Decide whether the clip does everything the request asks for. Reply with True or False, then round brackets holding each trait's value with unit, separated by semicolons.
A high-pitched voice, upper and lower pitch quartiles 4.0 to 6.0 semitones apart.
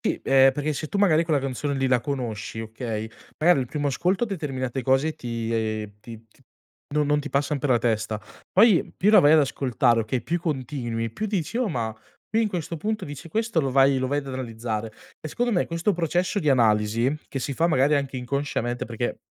False (135 Hz; 5.0 semitones)